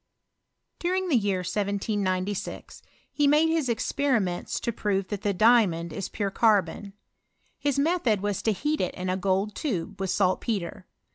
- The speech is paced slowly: No, average, 150 wpm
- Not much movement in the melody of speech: No, average, 4.6 semitones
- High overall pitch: Yes, high, 205 Hz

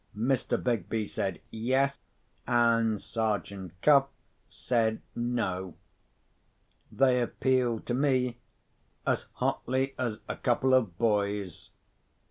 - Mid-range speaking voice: No, low, 115 Hz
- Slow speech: Yes, slow, 95 wpm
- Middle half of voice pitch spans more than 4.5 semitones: No, average, 3.6 semitones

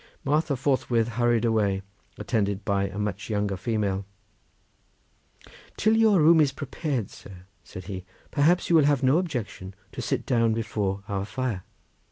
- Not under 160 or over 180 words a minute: No, average, 150 wpm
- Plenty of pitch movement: Yes, wide, 6.0 semitones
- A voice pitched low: Yes, low, 115 Hz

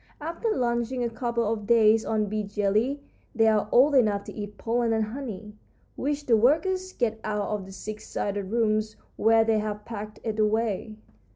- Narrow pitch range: Yes, narrow, 2.1 semitones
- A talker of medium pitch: No, high, 220 Hz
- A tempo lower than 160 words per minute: No, average, 180 wpm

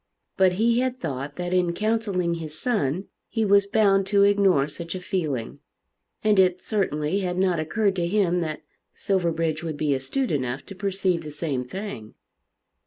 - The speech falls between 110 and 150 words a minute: No, average, 170 wpm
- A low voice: No, medium, 180 Hz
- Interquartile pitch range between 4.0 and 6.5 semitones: Yes, average, 4.5 semitones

